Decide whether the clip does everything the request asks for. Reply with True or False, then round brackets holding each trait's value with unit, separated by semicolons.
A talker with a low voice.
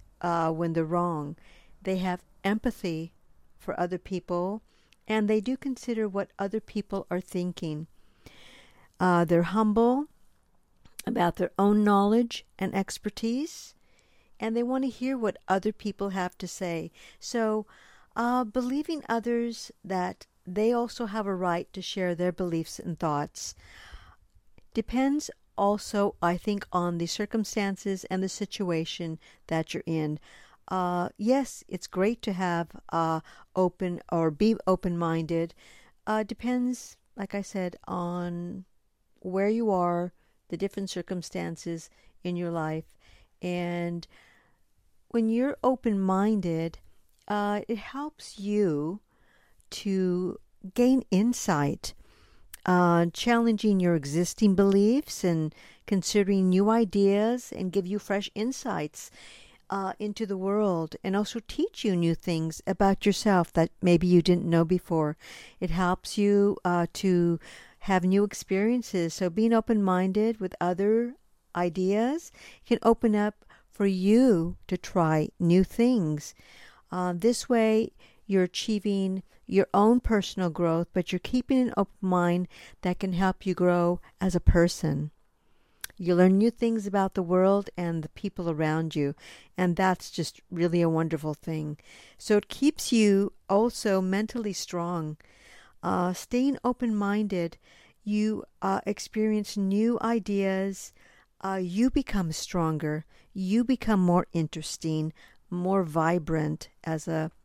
False (190 Hz)